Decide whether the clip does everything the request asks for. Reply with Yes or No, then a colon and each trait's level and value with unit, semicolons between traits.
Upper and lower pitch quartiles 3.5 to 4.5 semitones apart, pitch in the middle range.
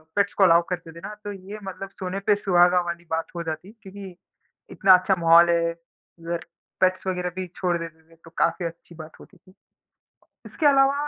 No: narrow, 2.5 semitones; medium, 180 Hz